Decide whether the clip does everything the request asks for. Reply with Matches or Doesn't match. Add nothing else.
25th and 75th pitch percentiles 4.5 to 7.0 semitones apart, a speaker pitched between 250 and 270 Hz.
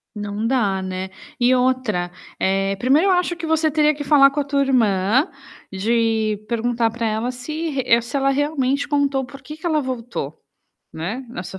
Matches